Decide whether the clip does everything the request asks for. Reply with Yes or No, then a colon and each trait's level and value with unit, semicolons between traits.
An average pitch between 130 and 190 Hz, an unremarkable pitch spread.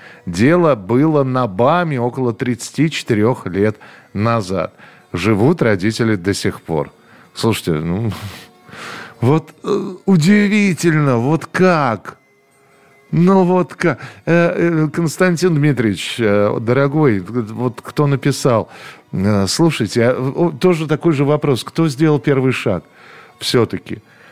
No: low, 135 Hz; wide, 6.1 semitones